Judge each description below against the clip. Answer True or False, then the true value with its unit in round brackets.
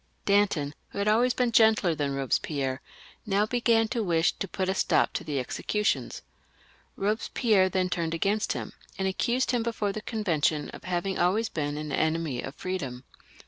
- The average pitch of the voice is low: False (190 Hz)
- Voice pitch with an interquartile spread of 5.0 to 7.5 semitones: True (5.5 semitones)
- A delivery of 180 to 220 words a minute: False (170 wpm)